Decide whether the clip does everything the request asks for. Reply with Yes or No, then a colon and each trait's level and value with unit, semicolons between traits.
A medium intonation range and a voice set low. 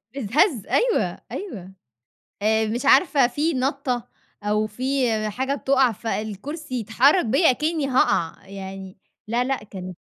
No: average, 4.8 semitones; high, 245 Hz